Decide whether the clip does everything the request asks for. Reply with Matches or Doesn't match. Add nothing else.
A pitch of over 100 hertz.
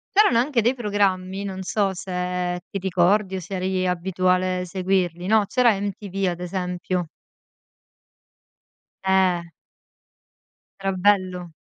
Matches